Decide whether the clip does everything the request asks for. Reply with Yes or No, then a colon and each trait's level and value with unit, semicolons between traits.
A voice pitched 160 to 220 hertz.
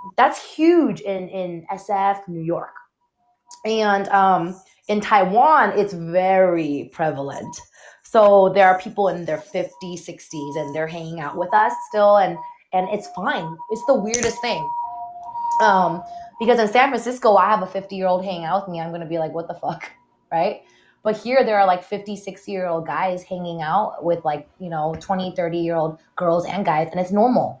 Yes: high, 190 Hz